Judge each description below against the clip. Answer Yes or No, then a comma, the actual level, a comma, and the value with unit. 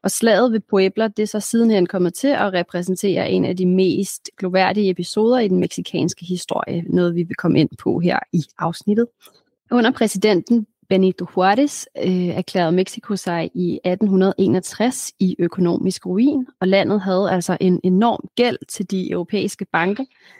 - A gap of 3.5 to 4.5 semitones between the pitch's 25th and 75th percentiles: No, average, 3.0 semitones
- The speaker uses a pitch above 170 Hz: Yes, high, 190 Hz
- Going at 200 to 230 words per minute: No, average, 160 wpm